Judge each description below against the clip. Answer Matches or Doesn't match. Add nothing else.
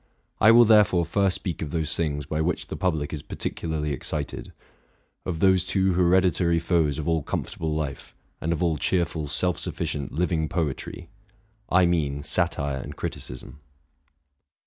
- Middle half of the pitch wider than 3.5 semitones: Doesn't match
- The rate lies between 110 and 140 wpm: Doesn't match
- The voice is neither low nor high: Doesn't match